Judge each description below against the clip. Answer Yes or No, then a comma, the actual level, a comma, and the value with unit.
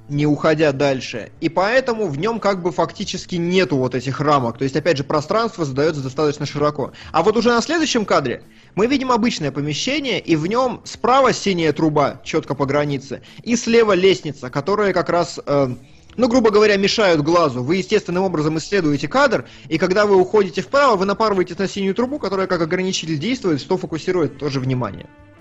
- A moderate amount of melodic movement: No, wide, 6.0 semitones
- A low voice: No, medium, 175 Hz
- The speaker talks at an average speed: No, fast, 180 wpm